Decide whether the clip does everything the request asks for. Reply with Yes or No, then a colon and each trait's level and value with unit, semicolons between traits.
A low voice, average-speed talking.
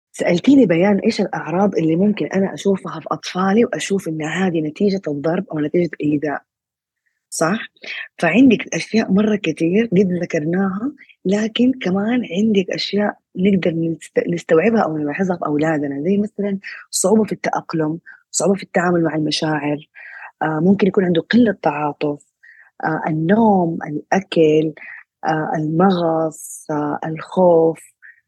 No: medium, 175 Hz; average, 125 wpm